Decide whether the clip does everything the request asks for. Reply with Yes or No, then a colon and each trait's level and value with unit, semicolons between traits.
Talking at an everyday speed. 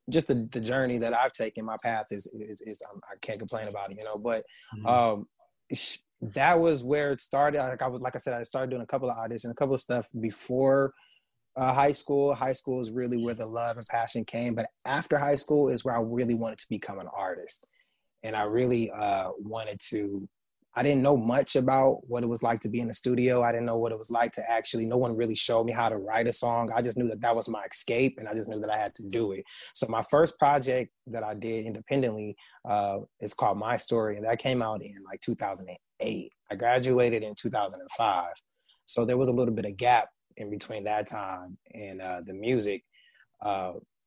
No: fast, 230 wpm